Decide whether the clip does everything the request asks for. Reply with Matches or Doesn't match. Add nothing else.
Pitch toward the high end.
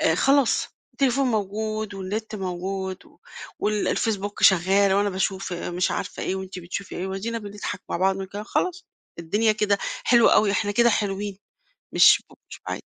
Matches